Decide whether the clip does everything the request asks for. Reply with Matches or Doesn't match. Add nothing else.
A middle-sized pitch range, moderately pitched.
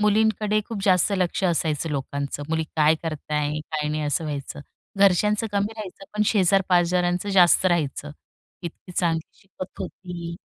Matches